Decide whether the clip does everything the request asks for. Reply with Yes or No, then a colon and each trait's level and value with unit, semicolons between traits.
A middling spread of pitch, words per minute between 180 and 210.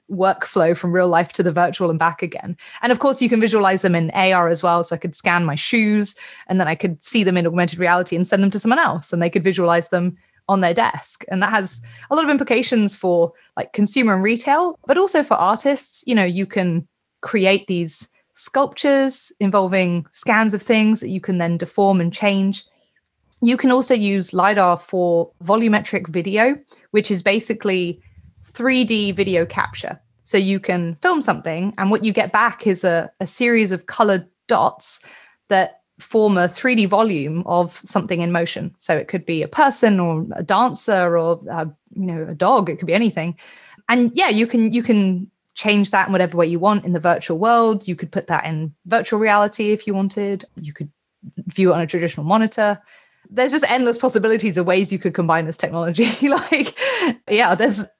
Yes: average, 4.1 semitones; average, 200 wpm